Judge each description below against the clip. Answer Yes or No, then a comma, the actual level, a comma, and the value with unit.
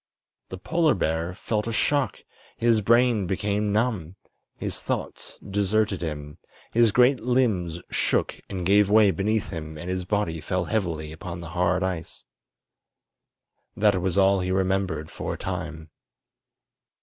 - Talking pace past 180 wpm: No, average, 140 wpm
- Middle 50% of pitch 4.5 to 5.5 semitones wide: No, average, 3.7 semitones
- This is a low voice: Yes, very low, 95 Hz